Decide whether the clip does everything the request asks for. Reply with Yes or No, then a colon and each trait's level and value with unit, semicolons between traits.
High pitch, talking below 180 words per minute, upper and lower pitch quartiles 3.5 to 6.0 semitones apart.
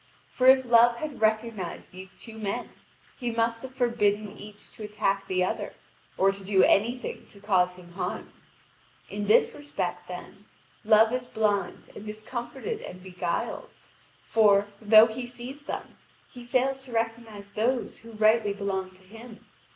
No: high, 220 Hz; average, 160 wpm; average, 3.1 semitones